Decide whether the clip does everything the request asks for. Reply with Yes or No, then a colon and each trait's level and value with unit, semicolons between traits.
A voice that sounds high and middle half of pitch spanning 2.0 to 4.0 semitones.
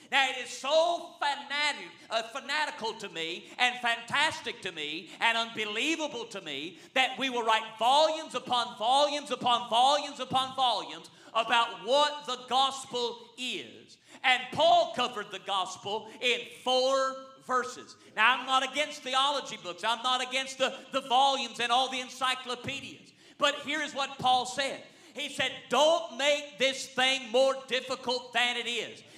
Yes: very high, 255 Hz; average, 2.9 semitones